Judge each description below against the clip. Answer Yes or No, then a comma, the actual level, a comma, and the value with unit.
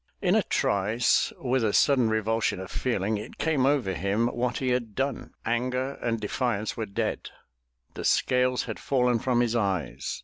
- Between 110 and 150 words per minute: No, average, 170 wpm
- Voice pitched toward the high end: No, low, 120 Hz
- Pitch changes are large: No, average, 3.1 semitones